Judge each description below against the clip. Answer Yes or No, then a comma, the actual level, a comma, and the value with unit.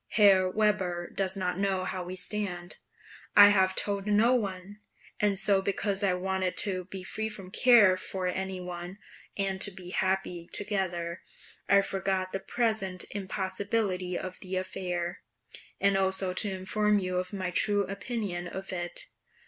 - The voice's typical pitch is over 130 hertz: Yes, high, 190 Hz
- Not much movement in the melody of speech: Yes, narrow, 1.7 semitones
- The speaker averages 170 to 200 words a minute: No, average, 155 wpm